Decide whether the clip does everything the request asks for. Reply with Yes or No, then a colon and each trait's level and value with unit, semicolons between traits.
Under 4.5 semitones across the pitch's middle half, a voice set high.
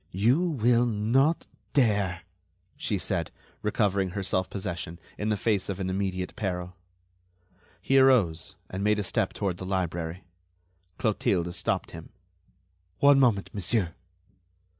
No: average, 3.9 semitones; low, 100 Hz